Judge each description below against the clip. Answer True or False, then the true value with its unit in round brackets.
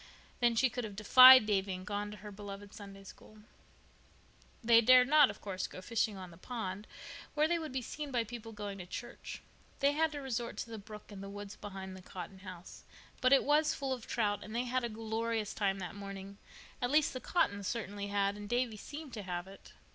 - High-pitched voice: True (215 Hz)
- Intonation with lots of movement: False (3.9 semitones)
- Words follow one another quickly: True (215 wpm)